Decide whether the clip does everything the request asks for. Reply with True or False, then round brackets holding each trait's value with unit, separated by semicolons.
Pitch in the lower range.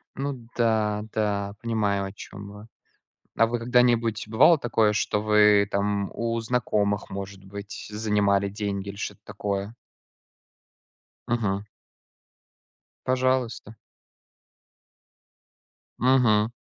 True (105 Hz)